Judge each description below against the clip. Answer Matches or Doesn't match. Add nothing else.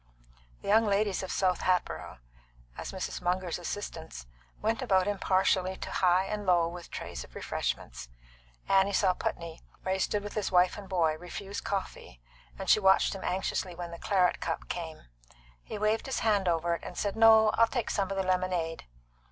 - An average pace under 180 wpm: Doesn't match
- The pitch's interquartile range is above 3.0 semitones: Doesn't match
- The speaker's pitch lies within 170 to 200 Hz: Matches